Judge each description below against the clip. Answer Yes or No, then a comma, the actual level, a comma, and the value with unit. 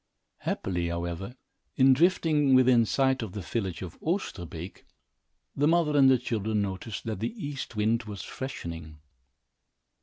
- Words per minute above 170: No, average, 140 wpm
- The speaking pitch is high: No, low, 115 Hz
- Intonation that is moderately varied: No, wide, 6.0 semitones